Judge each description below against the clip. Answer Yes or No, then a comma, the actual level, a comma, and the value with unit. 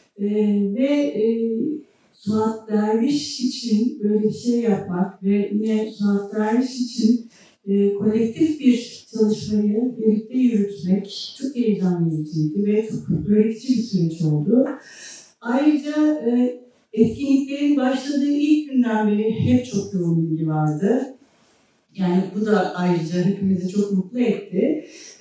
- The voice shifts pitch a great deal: No, average, 3.7 semitones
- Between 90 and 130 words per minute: Yes, average, 120 wpm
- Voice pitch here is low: No, high, 215 Hz